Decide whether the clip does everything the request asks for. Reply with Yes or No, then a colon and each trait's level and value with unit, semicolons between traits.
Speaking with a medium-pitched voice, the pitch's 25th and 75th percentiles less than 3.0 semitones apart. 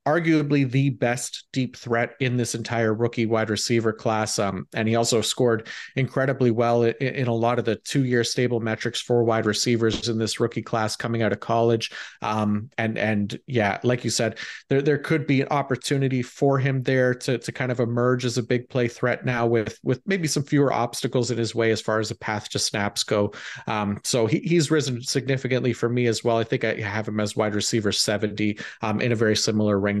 No: low, 120 Hz; narrow, 2.6 semitones